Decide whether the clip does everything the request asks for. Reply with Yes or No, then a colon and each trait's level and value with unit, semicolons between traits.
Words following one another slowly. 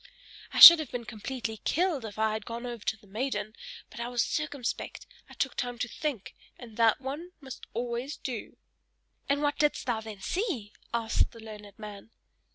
No: average, 185 wpm